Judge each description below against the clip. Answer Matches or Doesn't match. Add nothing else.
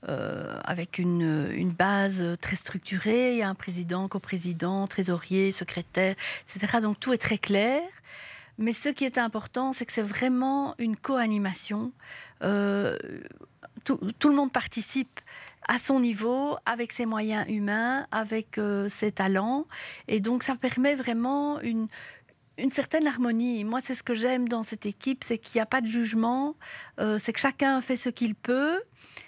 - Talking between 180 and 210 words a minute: Doesn't match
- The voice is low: Doesn't match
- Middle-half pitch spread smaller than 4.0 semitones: Doesn't match